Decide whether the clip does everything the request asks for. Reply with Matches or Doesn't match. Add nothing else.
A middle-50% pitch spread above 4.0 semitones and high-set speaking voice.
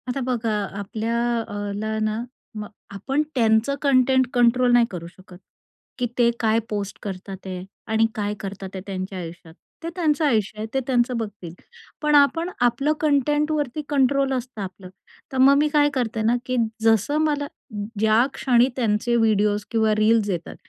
Matches